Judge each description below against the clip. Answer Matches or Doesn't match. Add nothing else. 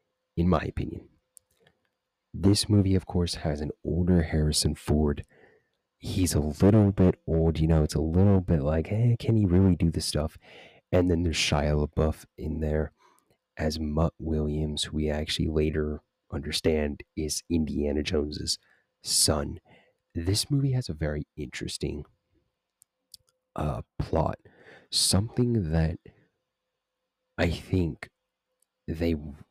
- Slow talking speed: Matches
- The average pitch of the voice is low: Matches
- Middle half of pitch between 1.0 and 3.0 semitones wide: Doesn't match